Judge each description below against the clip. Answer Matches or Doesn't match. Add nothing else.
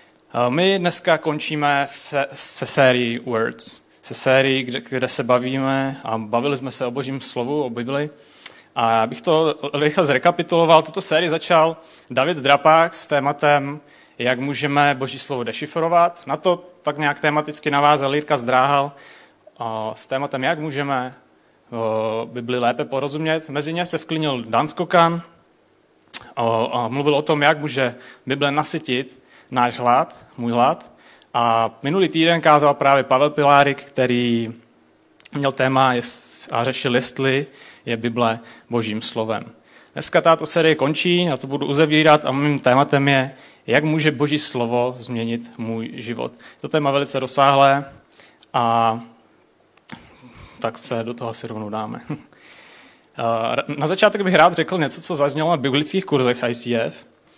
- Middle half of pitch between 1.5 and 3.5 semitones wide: Doesn't match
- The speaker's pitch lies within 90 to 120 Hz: Doesn't match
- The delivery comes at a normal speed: Matches